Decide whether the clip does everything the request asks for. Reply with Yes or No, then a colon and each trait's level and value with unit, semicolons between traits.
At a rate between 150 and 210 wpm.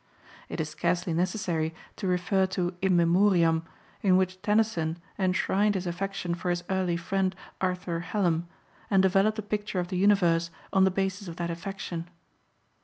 Yes: average, 160 wpm